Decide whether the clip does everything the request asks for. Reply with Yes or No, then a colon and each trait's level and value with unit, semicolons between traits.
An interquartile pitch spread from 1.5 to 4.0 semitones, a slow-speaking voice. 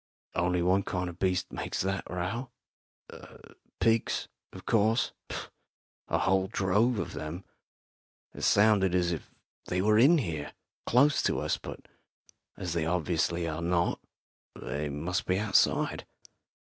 Yes: average, 3.4 semitones; slow, 130 wpm